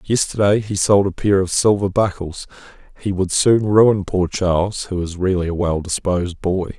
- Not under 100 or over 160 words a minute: No, average, 185 wpm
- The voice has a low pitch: Yes, very low, 95 Hz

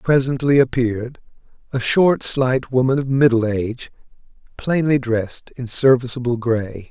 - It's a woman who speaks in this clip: No, male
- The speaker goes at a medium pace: No, slow, 120 wpm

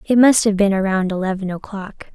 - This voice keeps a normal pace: Yes, average, 195 wpm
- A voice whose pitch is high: Yes, high, 200 Hz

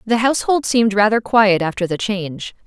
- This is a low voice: No, high, 210 Hz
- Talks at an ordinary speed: Yes, average, 180 wpm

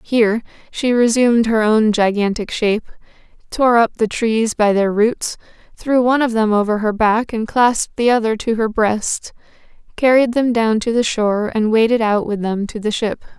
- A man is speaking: No, female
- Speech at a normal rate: Yes, average, 190 wpm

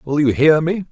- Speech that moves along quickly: Yes, fast, 265 wpm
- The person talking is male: Yes, male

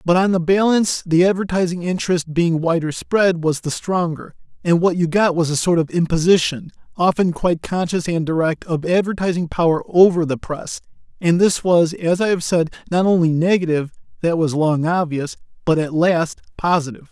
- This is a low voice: No, medium, 170 Hz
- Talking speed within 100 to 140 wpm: No, average, 180 wpm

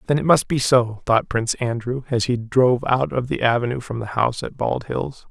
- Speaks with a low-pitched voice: Yes, low, 125 Hz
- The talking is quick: Yes, fast, 235 wpm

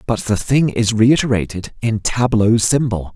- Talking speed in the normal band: Yes, average, 150 wpm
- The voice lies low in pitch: Yes, low, 115 Hz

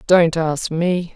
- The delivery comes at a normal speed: Yes, average, 155 wpm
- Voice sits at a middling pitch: Yes, medium, 170 Hz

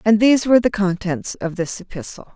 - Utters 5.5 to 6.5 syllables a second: Yes, 6.0 syllables/s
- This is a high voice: Yes, high, 200 Hz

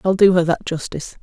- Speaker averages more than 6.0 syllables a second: Yes, 6.5 syllables/s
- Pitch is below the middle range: No, medium, 175 Hz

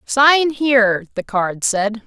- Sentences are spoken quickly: No, average, 145 wpm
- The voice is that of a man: No, female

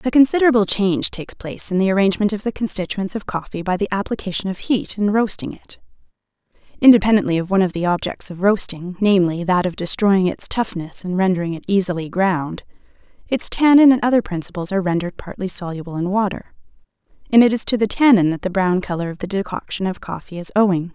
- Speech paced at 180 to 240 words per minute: Yes, average, 195 wpm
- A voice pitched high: Yes, high, 195 Hz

